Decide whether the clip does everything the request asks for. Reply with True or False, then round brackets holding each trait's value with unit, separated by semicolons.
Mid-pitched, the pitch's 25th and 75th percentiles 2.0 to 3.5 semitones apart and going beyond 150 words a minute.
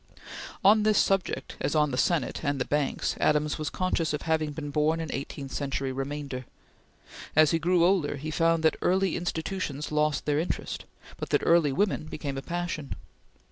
True (155 Hz; 2.8 semitones; 180 wpm)